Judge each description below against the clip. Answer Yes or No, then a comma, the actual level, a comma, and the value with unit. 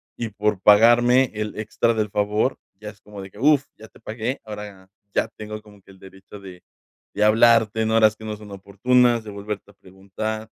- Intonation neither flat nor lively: No, narrow, 1.6 semitones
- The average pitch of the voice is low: Yes, low, 105 Hz